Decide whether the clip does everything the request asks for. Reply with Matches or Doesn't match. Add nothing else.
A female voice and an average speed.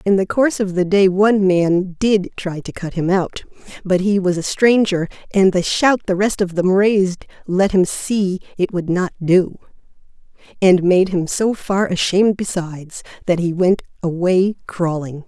Matches